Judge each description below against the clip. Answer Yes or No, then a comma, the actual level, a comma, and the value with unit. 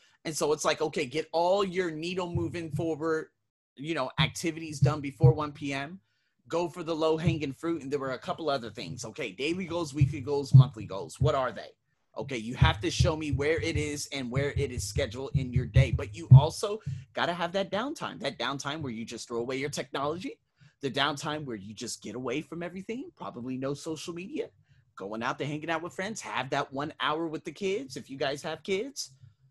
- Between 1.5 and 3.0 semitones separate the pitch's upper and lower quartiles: No, average, 3.5 semitones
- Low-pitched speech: No, medium, 150 Hz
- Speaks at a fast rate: Yes, fast, 215 wpm